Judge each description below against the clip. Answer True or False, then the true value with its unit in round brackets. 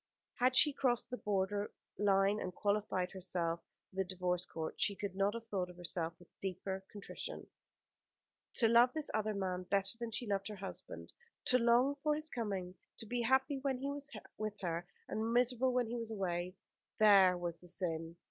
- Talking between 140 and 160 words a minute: False (185 wpm)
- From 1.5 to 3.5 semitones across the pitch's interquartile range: False (4.6 semitones)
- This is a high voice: True (205 Hz)